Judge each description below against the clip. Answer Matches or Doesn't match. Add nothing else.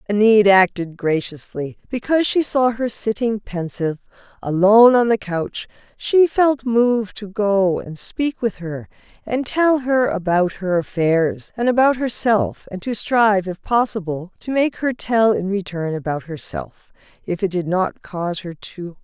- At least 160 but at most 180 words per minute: Matches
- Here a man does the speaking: Doesn't match